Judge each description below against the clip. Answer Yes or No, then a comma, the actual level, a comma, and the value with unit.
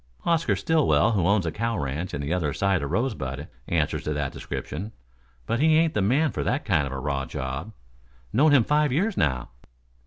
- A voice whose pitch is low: Yes, low, 100 Hz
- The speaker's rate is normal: No, fast, 210 wpm